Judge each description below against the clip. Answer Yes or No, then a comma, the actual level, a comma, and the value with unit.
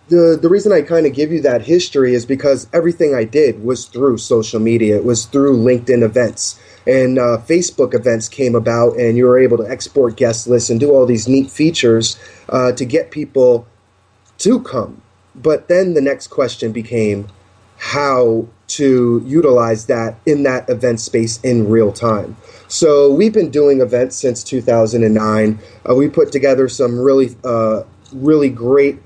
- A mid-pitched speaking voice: No, low, 125 Hz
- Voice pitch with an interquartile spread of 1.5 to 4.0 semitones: Yes, average, 3.4 semitones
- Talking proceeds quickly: No, average, 170 wpm